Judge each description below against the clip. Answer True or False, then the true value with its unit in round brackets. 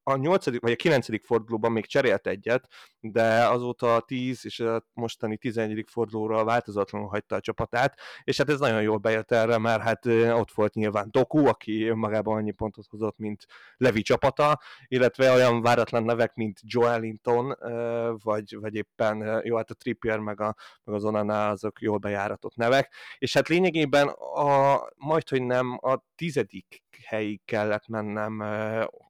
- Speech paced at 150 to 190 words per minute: True (155 wpm)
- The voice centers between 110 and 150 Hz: True (115 Hz)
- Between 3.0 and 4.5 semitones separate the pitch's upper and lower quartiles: False (2.4 semitones)